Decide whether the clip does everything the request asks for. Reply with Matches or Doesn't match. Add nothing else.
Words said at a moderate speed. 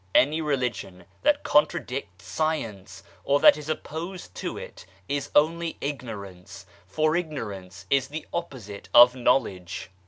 Doesn't match